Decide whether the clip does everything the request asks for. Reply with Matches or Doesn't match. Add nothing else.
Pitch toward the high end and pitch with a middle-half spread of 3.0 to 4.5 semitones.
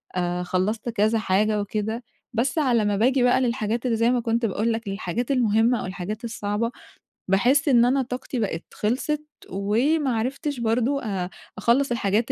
Matches